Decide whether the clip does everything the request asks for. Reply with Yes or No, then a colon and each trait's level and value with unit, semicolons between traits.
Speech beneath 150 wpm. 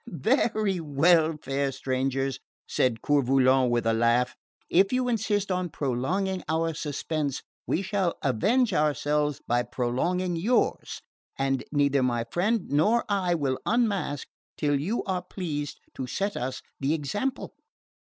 Yes: slow, 135 wpm